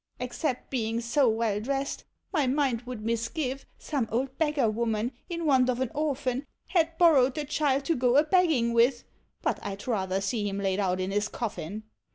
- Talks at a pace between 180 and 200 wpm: Yes, average, 195 wpm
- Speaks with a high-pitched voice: Yes, very high, 250 Hz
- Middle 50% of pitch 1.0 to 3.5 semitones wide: No, average, 4.3 semitones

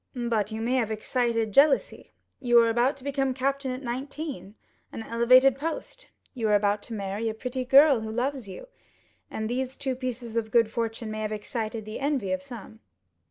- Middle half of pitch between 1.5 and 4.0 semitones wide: Yes, average, 3.3 semitones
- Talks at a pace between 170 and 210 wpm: Yes, average, 185 wpm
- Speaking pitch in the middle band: No, high, 240 Hz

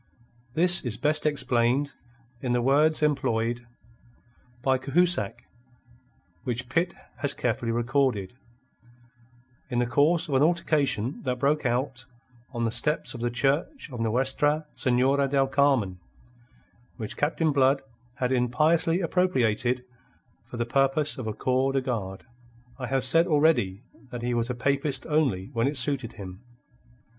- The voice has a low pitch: Yes, low, 130 Hz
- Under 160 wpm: Yes, average, 140 wpm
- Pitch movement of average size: Yes, average, 3.5 semitones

